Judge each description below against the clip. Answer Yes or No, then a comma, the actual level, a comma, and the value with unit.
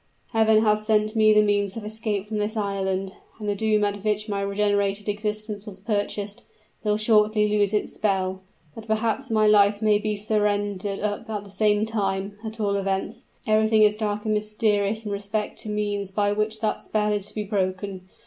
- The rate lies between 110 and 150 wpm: No, average, 190 wpm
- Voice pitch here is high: Yes, high, 210 Hz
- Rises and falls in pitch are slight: Yes, narrow, 1.1 semitones